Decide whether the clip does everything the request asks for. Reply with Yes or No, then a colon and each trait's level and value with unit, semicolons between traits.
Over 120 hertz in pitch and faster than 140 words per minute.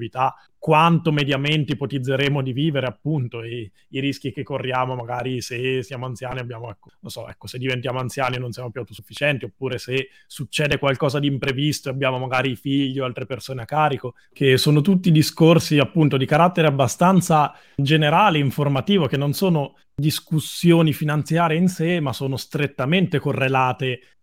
Yes: medium, 140 Hz; average, 160 wpm